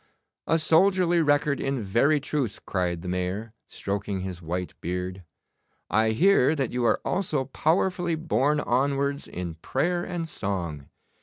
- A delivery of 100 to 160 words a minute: Yes, average, 140 wpm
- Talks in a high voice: No, low, 130 Hz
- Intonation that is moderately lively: No, wide, 9.0 semitones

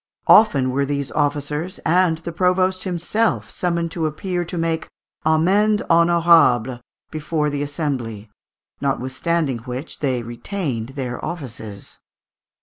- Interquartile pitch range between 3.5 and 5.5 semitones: Yes, average, 4.7 semitones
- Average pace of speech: No, slow, 115 wpm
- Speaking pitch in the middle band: Yes, medium, 155 Hz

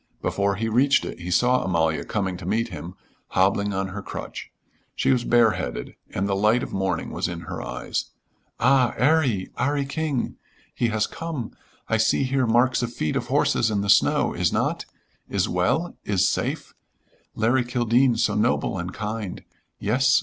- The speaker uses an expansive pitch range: No, average, 4.6 semitones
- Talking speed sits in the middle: Yes, average, 170 wpm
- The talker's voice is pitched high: No, low, 110 Hz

